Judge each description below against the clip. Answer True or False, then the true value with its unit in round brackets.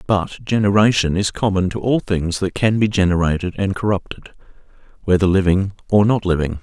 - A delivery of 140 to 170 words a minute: True (165 wpm)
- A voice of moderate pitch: False (95 Hz)